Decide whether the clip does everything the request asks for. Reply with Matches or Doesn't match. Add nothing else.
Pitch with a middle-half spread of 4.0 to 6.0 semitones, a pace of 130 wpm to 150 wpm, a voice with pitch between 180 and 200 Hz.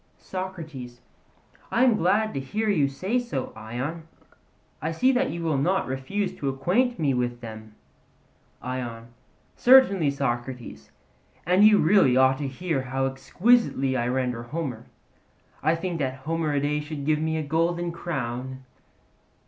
Doesn't match